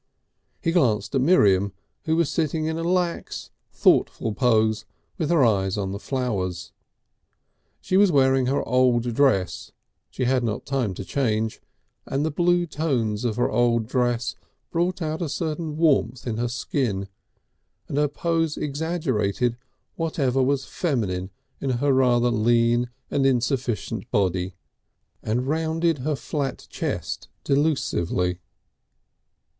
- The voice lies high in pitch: No, low, 130 Hz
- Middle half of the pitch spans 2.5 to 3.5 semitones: No, wide, 5.4 semitones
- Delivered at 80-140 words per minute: Yes, slow, 135 wpm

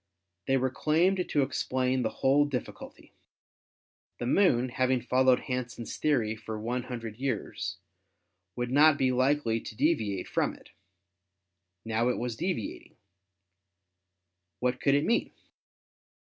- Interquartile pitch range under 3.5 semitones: Yes, average, 3.0 semitones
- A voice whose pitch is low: Yes, low, 125 Hz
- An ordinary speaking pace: No, slow, 130 wpm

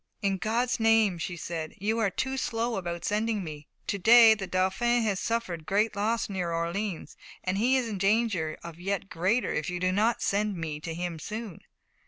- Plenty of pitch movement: No, average, 4.3 semitones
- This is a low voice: No, high, 200 Hz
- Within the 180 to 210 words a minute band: Yes, average, 195 wpm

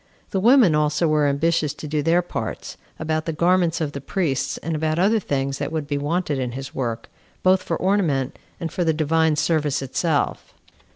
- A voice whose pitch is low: No, medium, 155 Hz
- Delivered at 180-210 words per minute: Yes, average, 190 wpm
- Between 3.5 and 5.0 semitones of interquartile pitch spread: No, average, 3.0 semitones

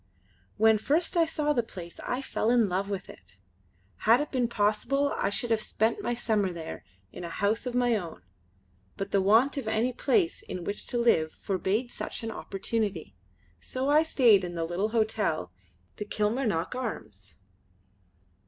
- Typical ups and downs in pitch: Yes, average, 4.4 semitones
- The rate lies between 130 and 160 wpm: No, average, 170 wpm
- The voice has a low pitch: No, high, 220 Hz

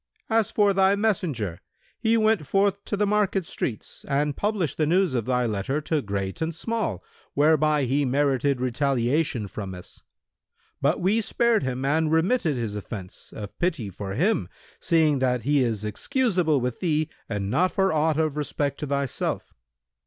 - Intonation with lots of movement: Yes, wide, 6.9 semitones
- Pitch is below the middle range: No, medium, 150 Hz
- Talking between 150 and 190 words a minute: Yes, average, 165 wpm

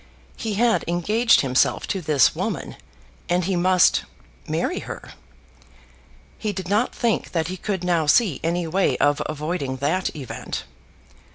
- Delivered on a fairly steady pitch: No, average, 4.1 semitones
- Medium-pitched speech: Yes, medium, 175 Hz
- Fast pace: No, average, 145 wpm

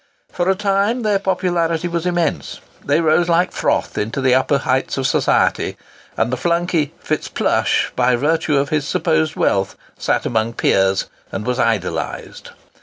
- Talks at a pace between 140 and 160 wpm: Yes, average, 155 wpm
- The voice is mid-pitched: Yes, medium, 155 Hz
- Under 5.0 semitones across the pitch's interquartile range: No, wide, 5.6 semitones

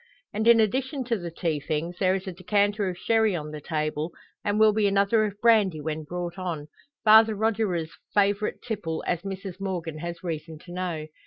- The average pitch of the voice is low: No, medium, 185 Hz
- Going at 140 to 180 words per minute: No, average, 190 wpm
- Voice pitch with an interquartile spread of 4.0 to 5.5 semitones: Yes, average, 4.4 semitones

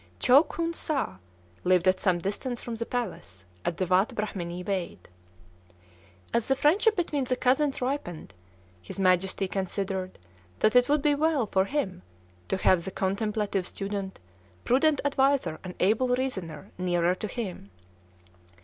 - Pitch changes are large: Yes, wide, 6.2 semitones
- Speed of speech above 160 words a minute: No, average, 145 wpm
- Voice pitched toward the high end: Yes, high, 205 Hz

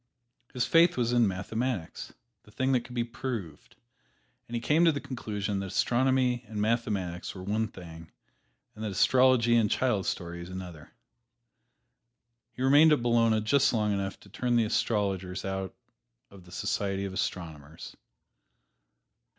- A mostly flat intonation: No, average, 4.4 semitones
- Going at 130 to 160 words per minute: Yes, average, 145 wpm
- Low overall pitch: Yes, low, 110 Hz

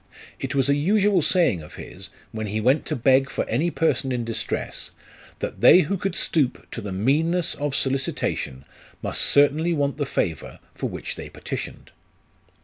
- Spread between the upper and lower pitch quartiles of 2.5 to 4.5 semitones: No, average, 5.3 semitones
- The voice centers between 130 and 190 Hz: Yes, medium, 140 Hz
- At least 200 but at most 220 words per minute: No, average, 170 wpm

